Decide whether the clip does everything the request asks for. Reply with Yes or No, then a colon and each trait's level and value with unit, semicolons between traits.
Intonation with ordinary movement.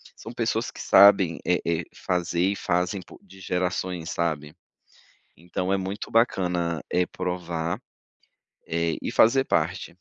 No: narrow, 1.9 semitones